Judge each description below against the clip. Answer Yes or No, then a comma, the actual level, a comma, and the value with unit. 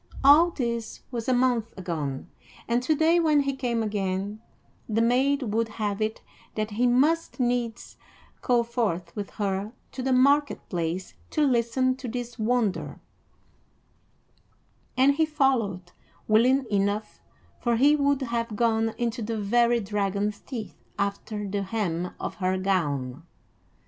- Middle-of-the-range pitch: No, high, 230 Hz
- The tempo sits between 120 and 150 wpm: Yes, average, 140 wpm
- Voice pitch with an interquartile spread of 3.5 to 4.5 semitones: Yes, average, 4.1 semitones